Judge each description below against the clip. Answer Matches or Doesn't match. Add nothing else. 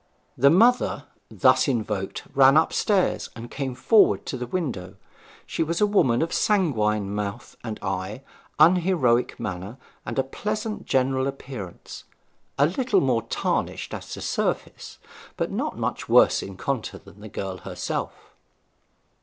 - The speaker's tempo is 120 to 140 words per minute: Matches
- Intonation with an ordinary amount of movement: Doesn't match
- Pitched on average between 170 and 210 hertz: Doesn't match